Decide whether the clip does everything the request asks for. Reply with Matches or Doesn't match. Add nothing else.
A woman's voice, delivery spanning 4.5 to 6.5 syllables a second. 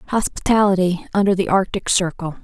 Matches